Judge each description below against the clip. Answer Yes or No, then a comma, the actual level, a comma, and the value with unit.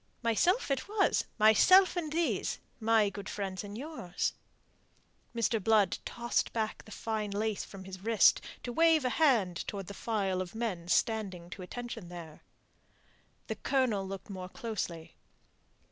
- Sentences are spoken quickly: No, average, 145 wpm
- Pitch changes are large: No, average, 4.0 semitones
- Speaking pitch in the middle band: No, high, 215 Hz